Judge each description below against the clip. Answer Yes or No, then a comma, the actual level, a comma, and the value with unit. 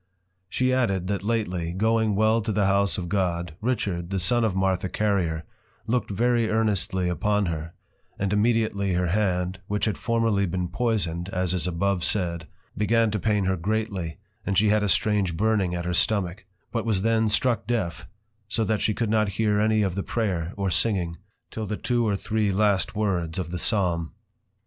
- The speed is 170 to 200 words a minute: Yes, average, 180 wpm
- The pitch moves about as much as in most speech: Yes, average, 3.3 semitones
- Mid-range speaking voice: No, low, 100 Hz